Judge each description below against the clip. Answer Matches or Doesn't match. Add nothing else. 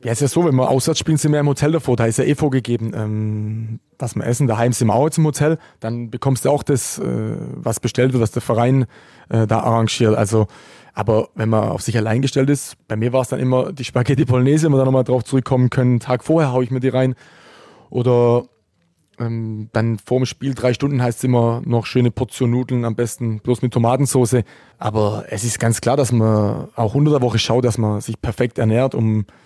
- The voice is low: Matches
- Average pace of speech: Doesn't match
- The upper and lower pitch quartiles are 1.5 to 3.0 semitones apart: Matches